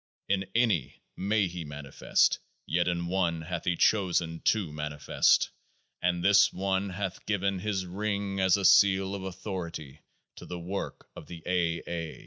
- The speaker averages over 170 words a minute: No, average, 155 wpm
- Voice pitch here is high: No, very low, 90 Hz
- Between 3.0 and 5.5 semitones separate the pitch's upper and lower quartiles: No, narrow, 2.5 semitones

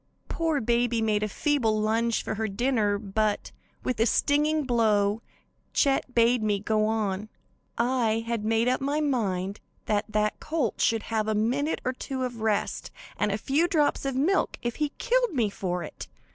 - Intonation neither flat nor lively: Yes, average, 4.0 semitones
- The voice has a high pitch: Yes, high, 230 Hz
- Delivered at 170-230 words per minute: Yes, average, 175 wpm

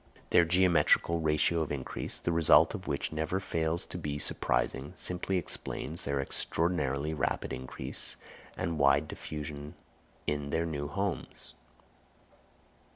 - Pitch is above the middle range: No, very low, 80 Hz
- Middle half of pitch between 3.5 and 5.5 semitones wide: No, average, 2.8 semitones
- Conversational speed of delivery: No, slow, 125 wpm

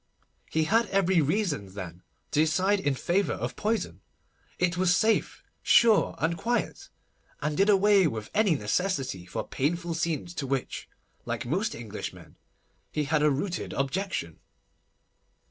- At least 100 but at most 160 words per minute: Yes, average, 140 wpm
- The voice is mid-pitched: Yes, medium, 170 Hz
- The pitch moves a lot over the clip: Yes, wide, 5.9 semitones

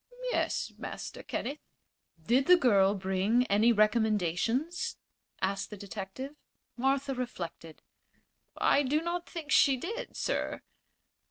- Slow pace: Yes, slow, 110 wpm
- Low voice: No, high, 240 Hz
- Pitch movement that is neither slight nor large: No, wide, 6.0 semitones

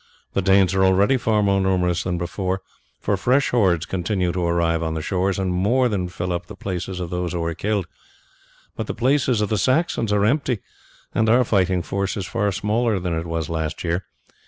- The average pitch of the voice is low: Yes, very low, 95 Hz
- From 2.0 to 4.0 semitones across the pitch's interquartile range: Yes, average, 3.1 semitones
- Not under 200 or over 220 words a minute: Yes, fast, 205 wpm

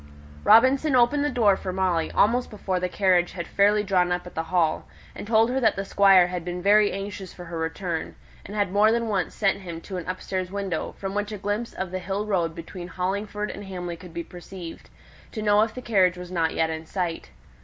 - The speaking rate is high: Yes, fast, 225 wpm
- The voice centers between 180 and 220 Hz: Yes, high, 190 Hz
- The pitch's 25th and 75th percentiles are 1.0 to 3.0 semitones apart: Yes, average, 2.7 semitones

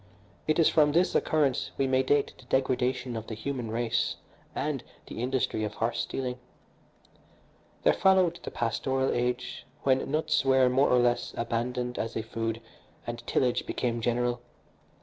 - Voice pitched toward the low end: Yes, low, 125 Hz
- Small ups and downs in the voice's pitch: Yes, narrow, 2.1 semitones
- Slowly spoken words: No, average, 155 wpm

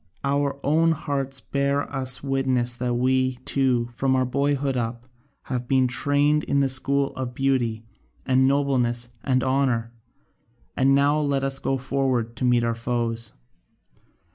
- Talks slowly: No, average, 145 wpm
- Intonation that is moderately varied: No, narrow, 2.1 semitones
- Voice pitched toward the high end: No, low, 130 Hz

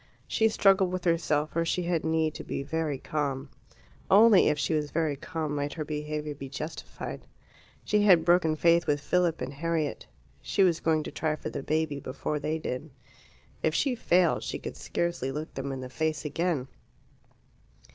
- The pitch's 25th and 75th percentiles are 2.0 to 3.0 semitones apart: Yes, average, 2.7 semitones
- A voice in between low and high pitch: Yes, medium, 155 Hz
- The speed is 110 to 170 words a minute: No, average, 180 wpm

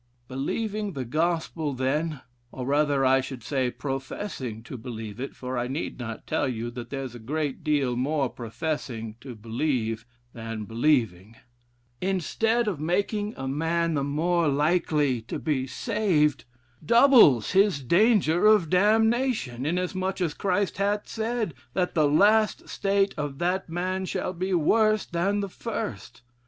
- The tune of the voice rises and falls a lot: Yes, wide, 6.7 semitones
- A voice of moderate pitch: Yes, medium, 155 Hz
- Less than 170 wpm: Yes, average, 145 wpm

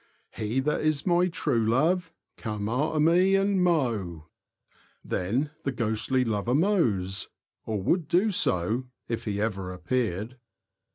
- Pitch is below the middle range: Yes, low, 125 Hz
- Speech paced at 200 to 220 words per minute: No, slow, 135 wpm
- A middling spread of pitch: No, wide, 7.7 semitones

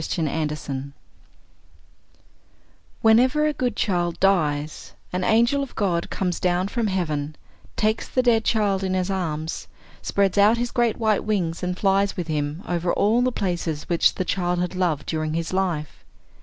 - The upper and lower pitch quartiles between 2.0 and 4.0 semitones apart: No, average, 4.7 semitones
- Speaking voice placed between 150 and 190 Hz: Yes, medium, 185 Hz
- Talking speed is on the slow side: No, average, 160 wpm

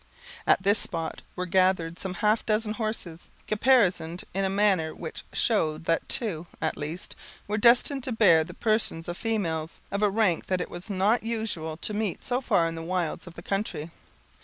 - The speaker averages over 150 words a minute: Yes, average, 185 wpm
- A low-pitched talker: No, high, 190 Hz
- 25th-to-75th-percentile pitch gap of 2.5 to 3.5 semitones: No, average, 4.5 semitones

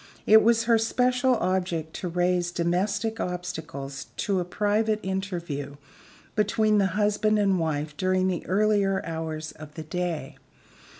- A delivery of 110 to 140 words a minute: Yes, slow, 135 wpm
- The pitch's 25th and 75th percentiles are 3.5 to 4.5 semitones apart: Yes, average, 4.1 semitones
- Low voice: No, medium, 185 Hz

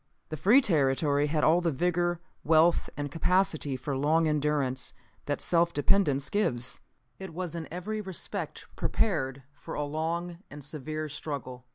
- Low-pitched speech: No, medium, 155 Hz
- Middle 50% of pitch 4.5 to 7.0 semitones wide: No, average, 3.3 semitones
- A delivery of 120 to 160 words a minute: Yes, average, 150 wpm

